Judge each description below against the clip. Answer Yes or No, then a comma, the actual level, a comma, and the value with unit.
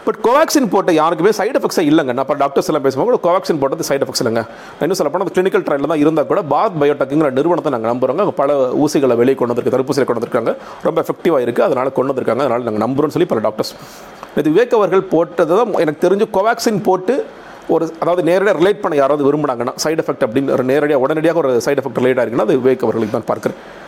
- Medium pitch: Yes, medium, 170 Hz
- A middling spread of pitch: No, wide, 7.0 semitones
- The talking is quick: Yes, fast, 195 wpm